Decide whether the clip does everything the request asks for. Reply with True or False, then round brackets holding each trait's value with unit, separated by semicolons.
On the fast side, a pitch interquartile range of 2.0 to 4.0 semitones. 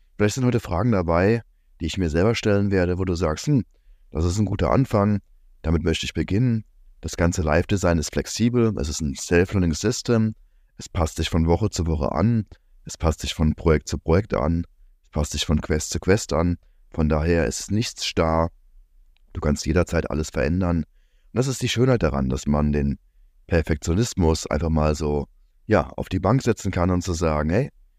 False (195 wpm; 4.6 semitones)